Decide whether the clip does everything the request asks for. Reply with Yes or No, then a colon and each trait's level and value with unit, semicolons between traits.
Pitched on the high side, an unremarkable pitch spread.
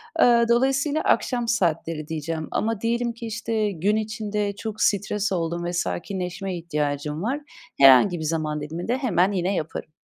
No: high, 195 Hz; wide, 5.7 semitones